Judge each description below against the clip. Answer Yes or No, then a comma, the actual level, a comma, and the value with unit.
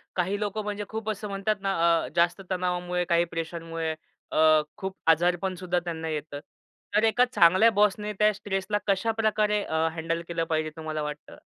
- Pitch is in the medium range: Yes, medium, 180 Hz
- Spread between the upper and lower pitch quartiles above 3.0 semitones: Yes, average, 3.9 semitones